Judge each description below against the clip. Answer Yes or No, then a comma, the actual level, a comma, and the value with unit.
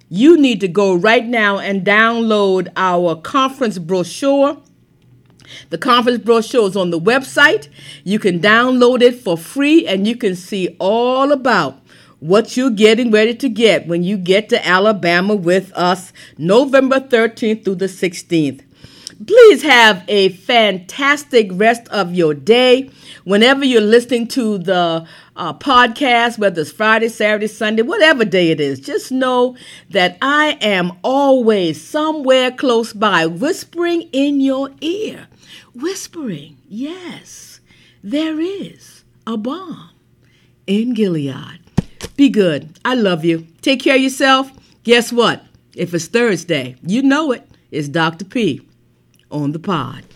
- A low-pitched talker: No, high, 220 Hz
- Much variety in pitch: Yes, wide, 6.3 semitones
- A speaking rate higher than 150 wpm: No, average, 140 wpm